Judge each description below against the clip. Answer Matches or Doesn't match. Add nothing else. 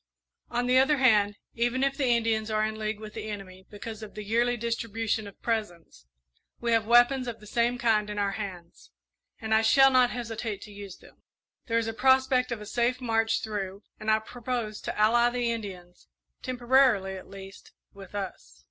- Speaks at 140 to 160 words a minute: Doesn't match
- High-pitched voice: Matches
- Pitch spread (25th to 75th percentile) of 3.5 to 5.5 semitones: Doesn't match